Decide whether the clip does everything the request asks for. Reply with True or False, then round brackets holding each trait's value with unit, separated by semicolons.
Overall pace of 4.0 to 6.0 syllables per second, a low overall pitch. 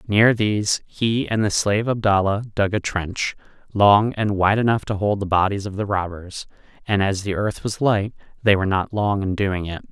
True (4.9 syllables/s; 100 Hz)